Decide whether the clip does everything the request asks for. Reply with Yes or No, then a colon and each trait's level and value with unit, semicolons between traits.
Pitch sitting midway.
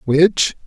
Yes: medium, 160 Hz